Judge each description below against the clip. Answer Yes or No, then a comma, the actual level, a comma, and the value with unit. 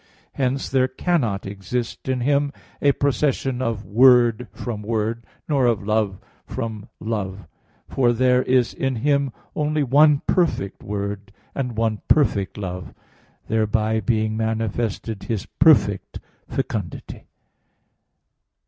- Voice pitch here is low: Yes, low, 115 Hz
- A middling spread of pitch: Yes, average, 3.9 semitones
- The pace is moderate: No, slow, 115 wpm